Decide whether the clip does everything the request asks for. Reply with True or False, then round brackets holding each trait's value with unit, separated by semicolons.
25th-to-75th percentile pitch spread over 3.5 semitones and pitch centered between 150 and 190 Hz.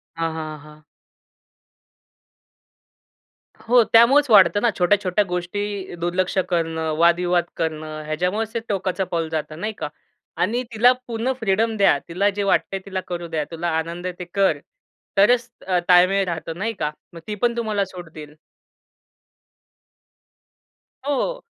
True (4.2 semitones; 185 Hz)